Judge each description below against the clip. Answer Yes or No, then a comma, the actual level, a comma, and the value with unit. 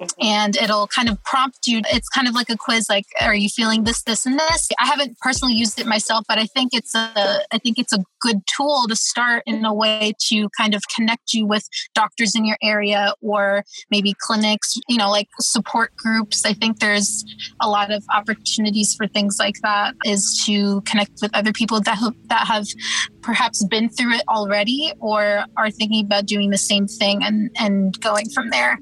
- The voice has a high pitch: Yes, high, 220 Hz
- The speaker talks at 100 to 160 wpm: No, fast, 205 wpm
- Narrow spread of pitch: Yes, narrow, 1.9 semitones